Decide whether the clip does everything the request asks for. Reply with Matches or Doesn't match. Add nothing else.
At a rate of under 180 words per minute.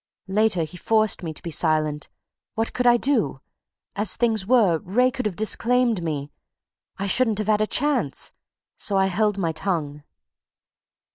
Matches